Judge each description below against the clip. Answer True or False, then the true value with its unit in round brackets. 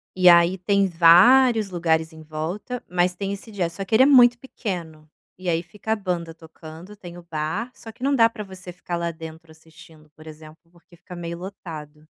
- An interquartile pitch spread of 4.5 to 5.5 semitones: False (3.7 semitones)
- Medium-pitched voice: True (175 Hz)